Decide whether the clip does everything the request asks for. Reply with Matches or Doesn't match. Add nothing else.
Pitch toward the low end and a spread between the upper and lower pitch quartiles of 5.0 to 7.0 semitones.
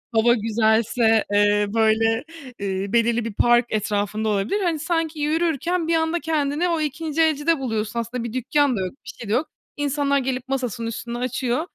Doesn't match